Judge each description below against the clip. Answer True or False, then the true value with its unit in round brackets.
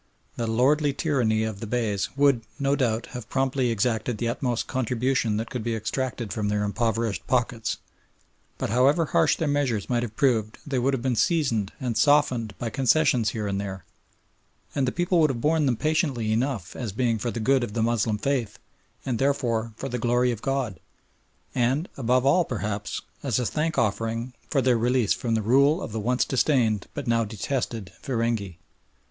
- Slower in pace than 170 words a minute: False (185 wpm)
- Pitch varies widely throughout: False (3.4 semitones)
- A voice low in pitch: True (120 Hz)